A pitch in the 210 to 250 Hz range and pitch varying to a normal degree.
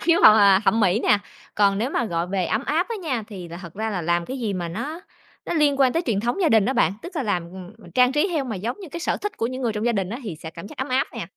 No: high, 220 Hz; wide, 6.1 semitones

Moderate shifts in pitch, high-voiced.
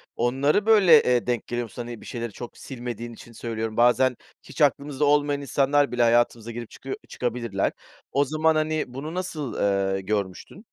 No: average, 3.7 semitones; low, 125 Hz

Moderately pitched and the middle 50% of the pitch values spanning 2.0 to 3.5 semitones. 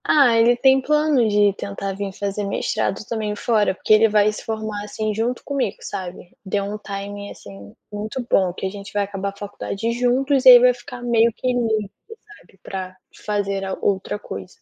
No: high, 210 Hz; average, 3.1 semitones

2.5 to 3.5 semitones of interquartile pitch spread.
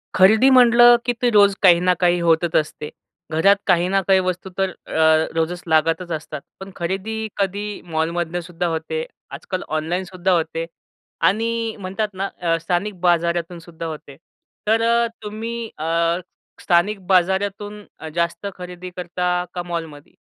Yes: average, 3.0 semitones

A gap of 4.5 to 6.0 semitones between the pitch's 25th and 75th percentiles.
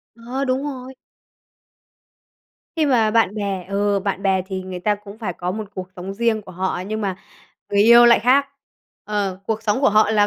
No: average, 3.3 semitones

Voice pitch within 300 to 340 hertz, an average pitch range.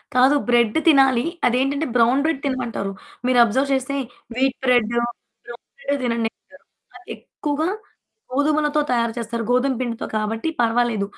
No: very high, 250 Hz; average, 3.1 semitones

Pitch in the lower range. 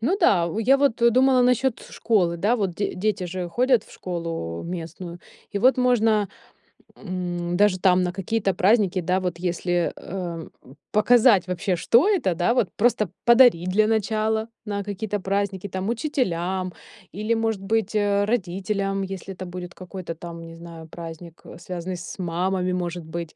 No: high, 190 Hz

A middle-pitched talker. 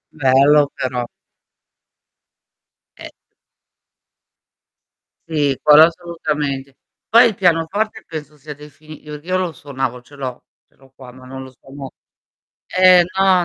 Yes: medium, 150 Hz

